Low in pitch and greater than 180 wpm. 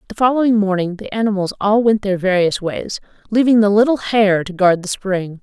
No: high, 200 Hz; average, 200 wpm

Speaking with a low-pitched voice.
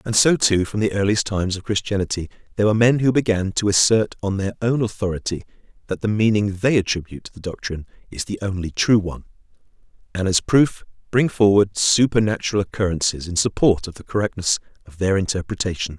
Yes: low, 100 Hz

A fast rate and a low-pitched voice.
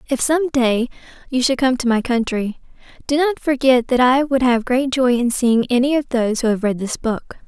No: fast, 225 wpm; very high, 250 Hz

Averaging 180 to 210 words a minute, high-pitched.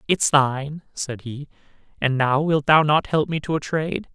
No: fast, 205 wpm; medium, 145 Hz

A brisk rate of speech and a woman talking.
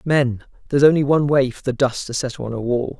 No: fast, 240 wpm; male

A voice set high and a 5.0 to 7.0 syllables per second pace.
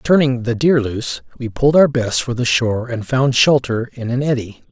No: low, 125 Hz; 5.2 syllables/s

